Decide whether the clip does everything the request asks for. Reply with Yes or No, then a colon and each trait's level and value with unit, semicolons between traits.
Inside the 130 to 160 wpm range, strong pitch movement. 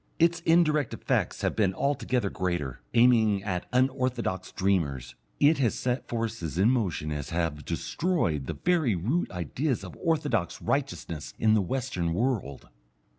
Yes: average, 145 wpm; wide, 7.3 semitones